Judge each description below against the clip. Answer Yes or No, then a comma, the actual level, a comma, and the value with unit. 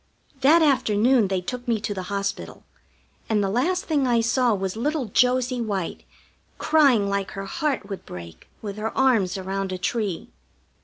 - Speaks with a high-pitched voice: Yes, high, 220 Hz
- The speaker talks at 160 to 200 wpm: Yes, average, 165 wpm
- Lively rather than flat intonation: No, average, 4.6 semitones